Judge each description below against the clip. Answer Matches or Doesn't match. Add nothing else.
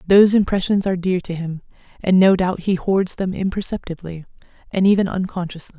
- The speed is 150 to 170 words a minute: Matches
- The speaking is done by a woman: Matches